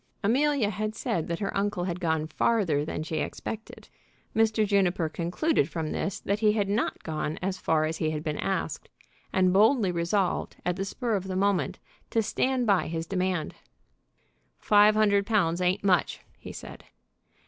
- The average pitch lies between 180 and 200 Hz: Yes, high, 190 Hz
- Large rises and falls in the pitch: No, average, 3.9 semitones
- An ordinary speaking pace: Yes, average, 170 wpm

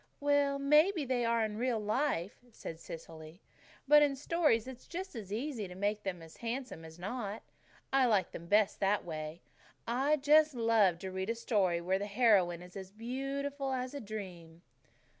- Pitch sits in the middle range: No, high, 225 Hz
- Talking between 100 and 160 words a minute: No, average, 170 wpm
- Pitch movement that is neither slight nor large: No, wide, 6.3 semitones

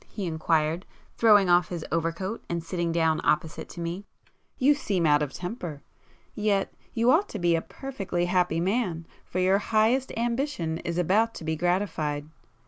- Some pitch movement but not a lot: Yes, average, 4.3 semitones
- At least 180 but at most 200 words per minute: No, average, 155 wpm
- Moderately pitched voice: Yes, medium, 180 Hz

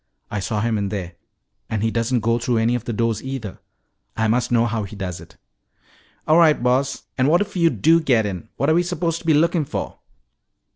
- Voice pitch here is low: Yes, low, 120 Hz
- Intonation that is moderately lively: No, wide, 6.0 semitones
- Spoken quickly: Yes, fast, 225 wpm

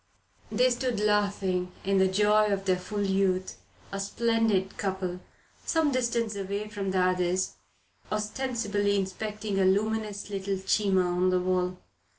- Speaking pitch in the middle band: No, high, 200 Hz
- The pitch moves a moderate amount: No, narrow, 2.1 semitones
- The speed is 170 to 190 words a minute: No, average, 140 wpm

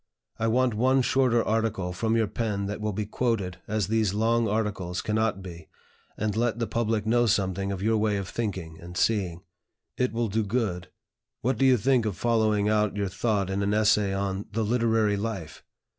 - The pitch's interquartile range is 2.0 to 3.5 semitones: Yes, narrow, 2.5 semitones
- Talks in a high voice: No, low, 105 Hz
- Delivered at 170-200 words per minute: Yes, average, 190 wpm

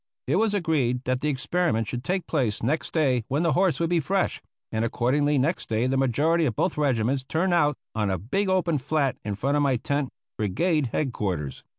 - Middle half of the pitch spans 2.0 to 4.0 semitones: No, average, 5.2 semitones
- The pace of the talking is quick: Yes, fast, 210 wpm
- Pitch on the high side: No, medium, 140 Hz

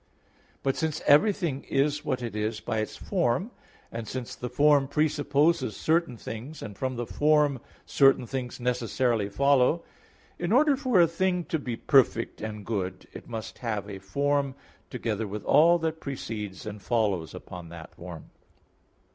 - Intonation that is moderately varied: No, wide, 5.8 semitones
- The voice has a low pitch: Yes, low, 130 Hz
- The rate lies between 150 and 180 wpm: Yes, average, 155 wpm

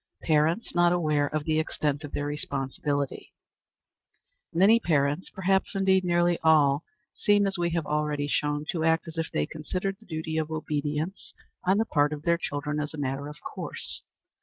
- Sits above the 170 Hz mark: No, medium, 155 Hz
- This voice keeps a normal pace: Yes, average, 175 wpm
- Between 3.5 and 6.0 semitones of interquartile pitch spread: No, average, 2.9 semitones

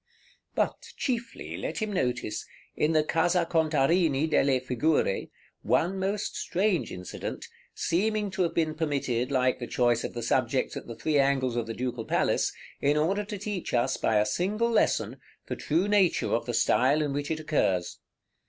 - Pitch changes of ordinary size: No, wide, 6.3 semitones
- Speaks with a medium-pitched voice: Yes, medium, 150 Hz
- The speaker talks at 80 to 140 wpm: No, average, 170 wpm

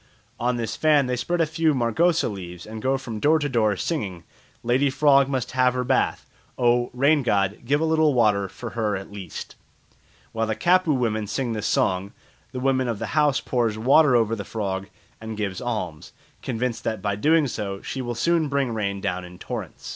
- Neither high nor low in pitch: No, low, 120 Hz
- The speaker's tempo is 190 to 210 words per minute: Yes, average, 200 wpm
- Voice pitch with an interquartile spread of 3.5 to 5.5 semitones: Yes, average, 4.8 semitones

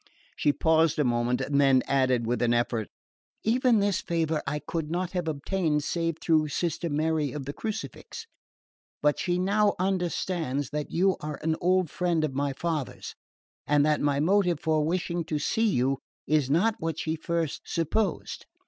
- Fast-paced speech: No, average, 175 wpm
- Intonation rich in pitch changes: No, average, 3.7 semitones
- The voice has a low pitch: No, medium, 160 Hz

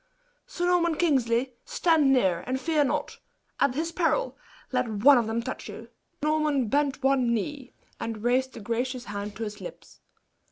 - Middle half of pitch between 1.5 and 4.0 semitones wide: No, average, 4.5 semitones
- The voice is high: Yes, very high, 260 Hz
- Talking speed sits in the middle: Yes, average, 175 wpm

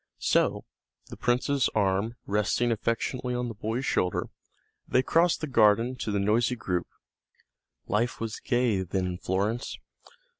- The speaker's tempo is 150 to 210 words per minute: No, average, 140 wpm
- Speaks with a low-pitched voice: Yes, low, 115 Hz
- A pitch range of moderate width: Yes, average, 3.4 semitones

